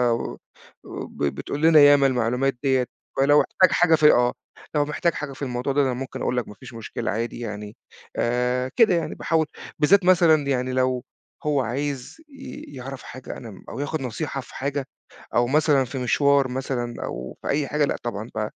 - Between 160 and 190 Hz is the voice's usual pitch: No, low, 135 Hz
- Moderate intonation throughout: Yes, average, 3.1 semitones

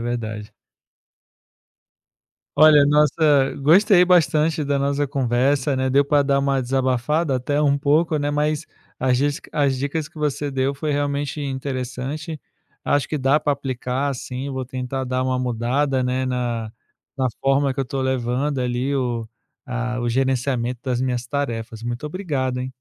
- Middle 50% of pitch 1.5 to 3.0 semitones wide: Yes, narrow, 2.4 semitones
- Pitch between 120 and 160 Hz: Yes, low, 135 Hz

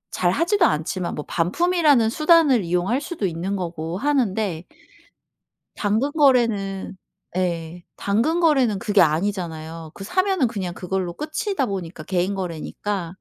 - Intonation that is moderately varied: No, wide, 7.7 semitones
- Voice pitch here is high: Yes, high, 195 Hz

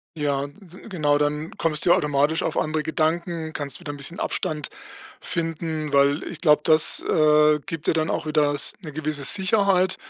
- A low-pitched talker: No, medium, 155 Hz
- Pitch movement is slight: Yes, narrow, 2.0 semitones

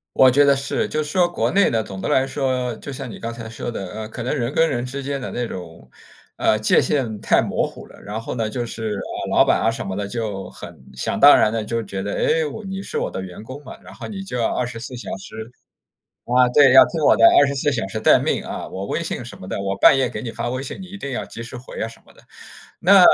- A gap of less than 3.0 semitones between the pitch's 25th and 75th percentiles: No, average, 4.2 semitones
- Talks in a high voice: No, low, 120 Hz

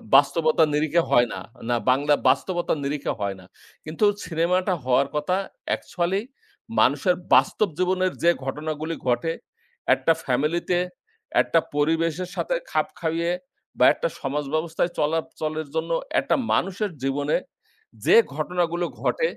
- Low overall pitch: No, medium, 165 Hz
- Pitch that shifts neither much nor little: Yes, average, 3.2 semitones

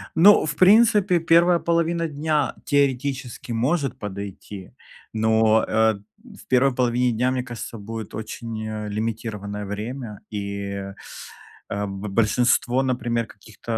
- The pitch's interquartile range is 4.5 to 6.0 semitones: Yes, average, 4.8 semitones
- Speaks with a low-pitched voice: Yes, low, 115 Hz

